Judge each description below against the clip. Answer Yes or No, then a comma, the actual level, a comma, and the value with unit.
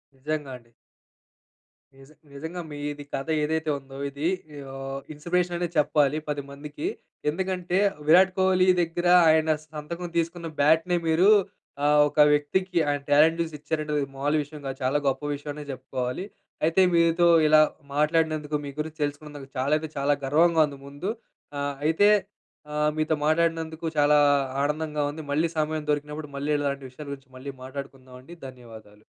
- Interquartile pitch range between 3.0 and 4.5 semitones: No, narrow, 2.5 semitones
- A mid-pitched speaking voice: Yes, medium, 150 Hz